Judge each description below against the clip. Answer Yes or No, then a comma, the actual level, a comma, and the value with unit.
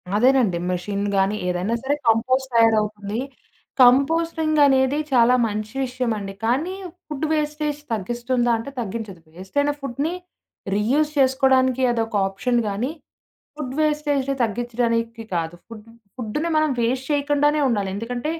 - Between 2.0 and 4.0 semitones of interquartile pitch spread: No, average, 4.6 semitones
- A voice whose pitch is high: Yes, high, 245 Hz